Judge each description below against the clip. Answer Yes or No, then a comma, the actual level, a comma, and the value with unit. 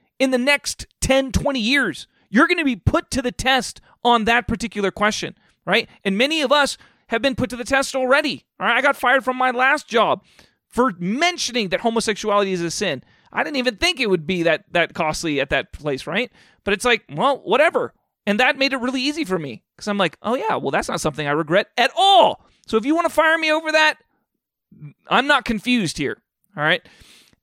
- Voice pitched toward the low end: No, high, 240 Hz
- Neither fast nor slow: No, fast, 220 wpm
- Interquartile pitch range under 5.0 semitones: No, wide, 5.5 semitones